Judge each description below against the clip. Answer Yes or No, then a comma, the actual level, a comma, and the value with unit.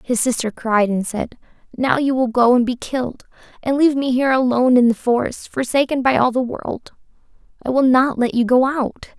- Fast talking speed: Yes, fast, 210 wpm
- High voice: Yes, very high, 250 Hz